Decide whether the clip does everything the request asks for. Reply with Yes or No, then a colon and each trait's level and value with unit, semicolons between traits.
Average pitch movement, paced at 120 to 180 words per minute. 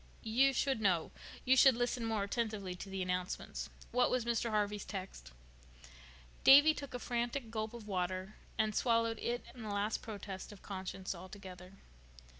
Yes: average, 3.8 semitones; average, 160 wpm